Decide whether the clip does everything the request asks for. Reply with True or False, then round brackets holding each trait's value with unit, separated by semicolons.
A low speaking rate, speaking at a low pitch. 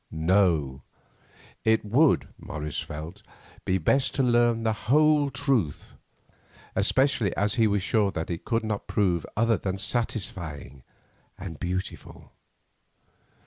True (120 wpm; 105 Hz)